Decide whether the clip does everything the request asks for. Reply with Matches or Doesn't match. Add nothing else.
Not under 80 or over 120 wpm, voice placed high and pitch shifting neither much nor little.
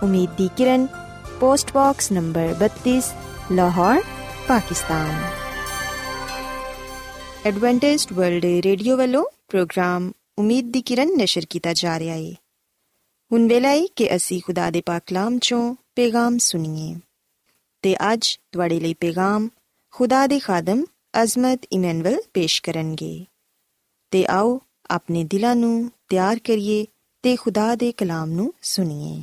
Doesn't match